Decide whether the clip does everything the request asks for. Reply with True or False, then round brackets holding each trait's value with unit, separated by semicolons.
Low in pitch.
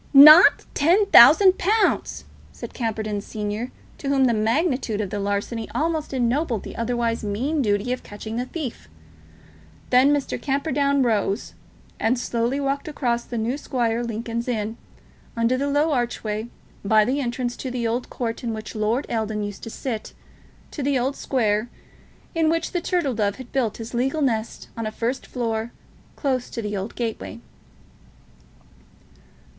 False (240 Hz)